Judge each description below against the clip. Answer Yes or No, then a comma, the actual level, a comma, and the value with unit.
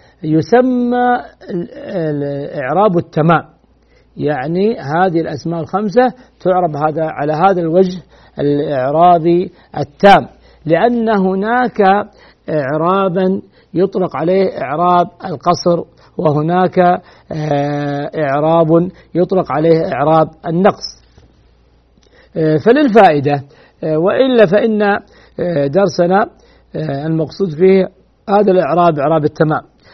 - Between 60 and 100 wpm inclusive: Yes, average, 75 wpm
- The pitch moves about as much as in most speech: Yes, average, 3.9 semitones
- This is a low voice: No, medium, 175 Hz